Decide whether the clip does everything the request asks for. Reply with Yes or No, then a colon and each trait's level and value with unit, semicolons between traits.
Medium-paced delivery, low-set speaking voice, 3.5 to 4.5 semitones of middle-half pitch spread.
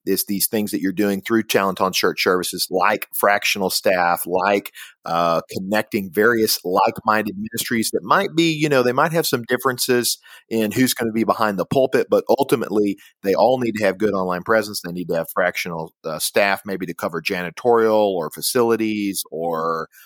Yes: average, 185 wpm; low, 110 Hz; average, 4.2 semitones